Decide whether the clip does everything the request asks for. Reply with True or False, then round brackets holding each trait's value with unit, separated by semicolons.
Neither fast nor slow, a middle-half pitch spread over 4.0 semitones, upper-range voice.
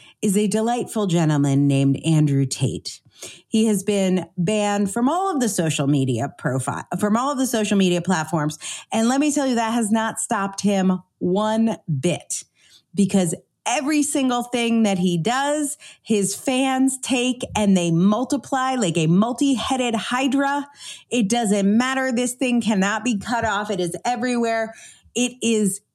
True (155 wpm; 5.3 semitones; 215 Hz)